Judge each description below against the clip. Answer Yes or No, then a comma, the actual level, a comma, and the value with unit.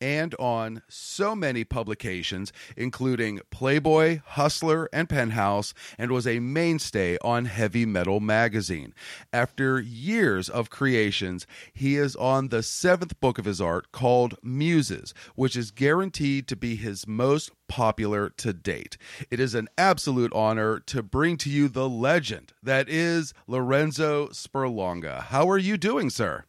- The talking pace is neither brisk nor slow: Yes, average, 145 wpm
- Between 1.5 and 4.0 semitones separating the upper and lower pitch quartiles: No, average, 4.7 semitones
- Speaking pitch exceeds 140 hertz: No, low, 125 Hz